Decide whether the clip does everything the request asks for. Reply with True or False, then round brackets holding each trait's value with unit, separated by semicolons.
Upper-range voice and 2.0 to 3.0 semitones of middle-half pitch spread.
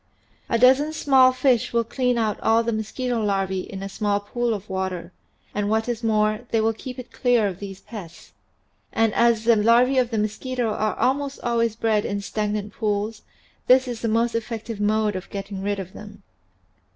True (220 Hz; 2.7 semitones)